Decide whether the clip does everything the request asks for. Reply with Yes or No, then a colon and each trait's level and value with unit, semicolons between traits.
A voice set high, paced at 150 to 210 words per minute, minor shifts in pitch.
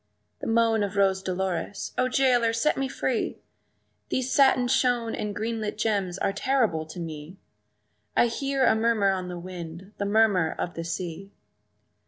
No: high, 210 Hz; average, 165 wpm; average, 4.2 semitones